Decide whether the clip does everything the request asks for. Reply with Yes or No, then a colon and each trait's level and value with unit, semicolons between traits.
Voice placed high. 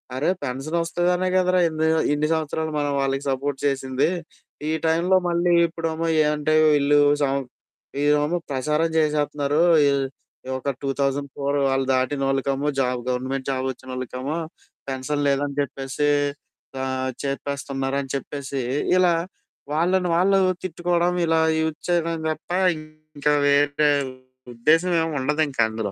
No: medium, 145 Hz